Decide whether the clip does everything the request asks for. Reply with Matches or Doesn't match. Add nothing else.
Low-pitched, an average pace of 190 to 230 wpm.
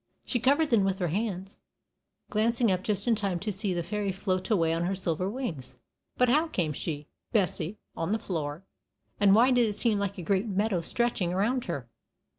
Doesn't match